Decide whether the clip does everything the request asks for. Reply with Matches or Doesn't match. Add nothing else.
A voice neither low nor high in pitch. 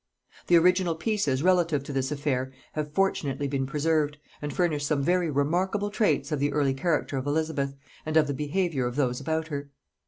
Matches